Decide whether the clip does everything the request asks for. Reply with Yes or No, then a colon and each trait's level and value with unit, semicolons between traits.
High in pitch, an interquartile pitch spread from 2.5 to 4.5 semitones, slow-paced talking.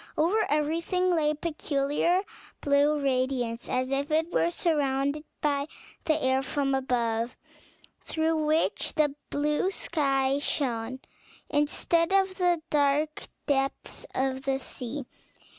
Yes: very high, 290 Hz; average, 2.9 semitones; slow, 120 wpm